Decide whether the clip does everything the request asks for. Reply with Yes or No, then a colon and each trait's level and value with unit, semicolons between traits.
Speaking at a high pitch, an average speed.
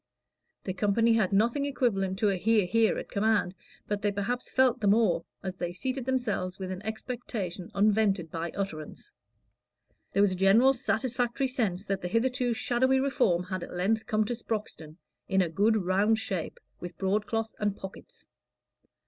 Yes: high, 210 Hz; average, 165 wpm